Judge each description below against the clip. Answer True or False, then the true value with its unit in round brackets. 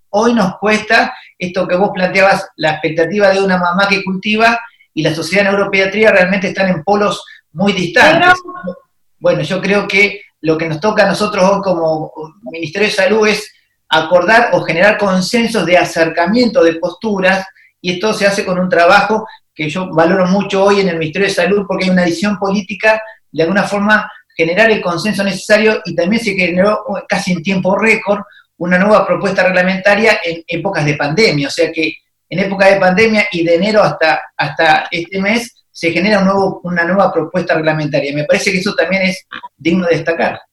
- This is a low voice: False (190 Hz)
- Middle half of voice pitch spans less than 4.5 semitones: True (3.0 semitones)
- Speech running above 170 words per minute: True (185 wpm)